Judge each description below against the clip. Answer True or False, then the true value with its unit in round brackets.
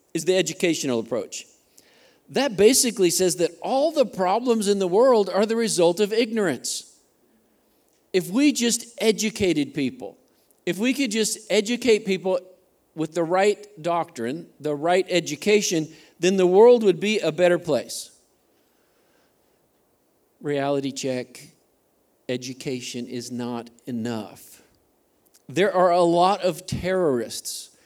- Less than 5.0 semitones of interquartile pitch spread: False (5.6 semitones)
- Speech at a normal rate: False (125 wpm)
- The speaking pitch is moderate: True (180 Hz)